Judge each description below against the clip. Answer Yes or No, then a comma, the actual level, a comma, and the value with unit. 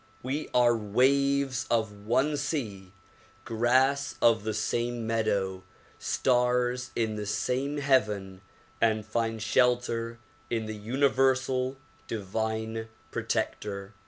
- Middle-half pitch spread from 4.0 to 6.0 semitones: No, average, 3.1 semitones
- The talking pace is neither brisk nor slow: No, slow, 100 wpm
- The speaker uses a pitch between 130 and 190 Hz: No, low, 115 Hz